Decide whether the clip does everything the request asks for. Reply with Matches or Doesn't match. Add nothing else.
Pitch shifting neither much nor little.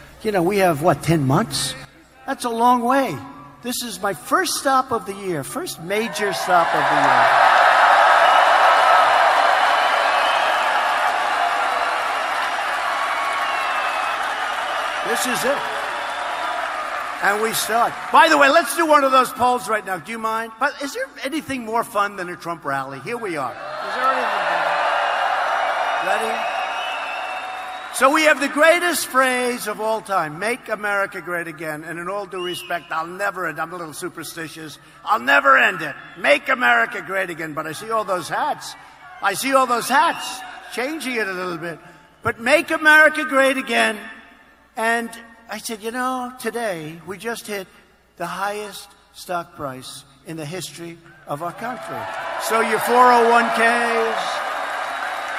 Doesn't match